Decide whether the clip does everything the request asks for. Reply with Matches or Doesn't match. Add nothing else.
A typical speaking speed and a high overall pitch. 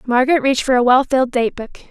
Doesn't match